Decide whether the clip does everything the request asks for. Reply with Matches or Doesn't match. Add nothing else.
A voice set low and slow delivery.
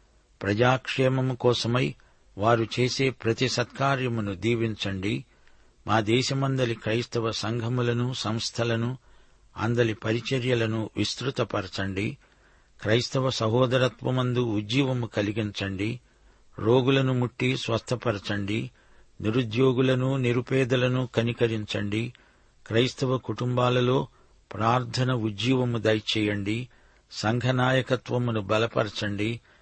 Matches